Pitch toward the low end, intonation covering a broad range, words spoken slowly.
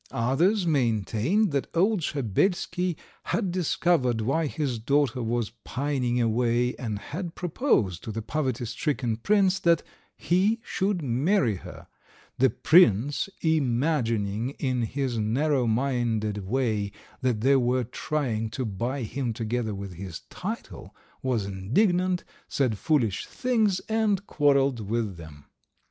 Yes: low, 130 Hz; wide, 6.3 semitones; slow, 125 wpm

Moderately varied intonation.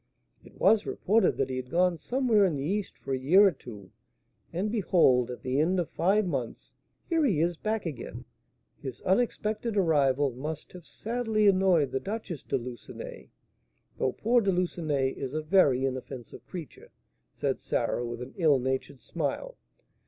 No: wide, 7.2 semitones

